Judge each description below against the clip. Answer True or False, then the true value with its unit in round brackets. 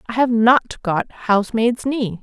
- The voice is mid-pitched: False (230 Hz)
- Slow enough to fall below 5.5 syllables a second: True (3.8 syllables/s)